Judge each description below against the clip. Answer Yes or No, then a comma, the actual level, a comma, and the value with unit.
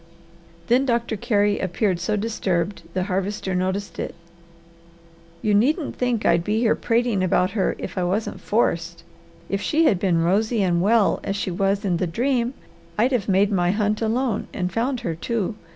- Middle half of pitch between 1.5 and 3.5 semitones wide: No, average, 3.9 semitones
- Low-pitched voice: No, high, 205 Hz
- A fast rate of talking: No, average, 175 wpm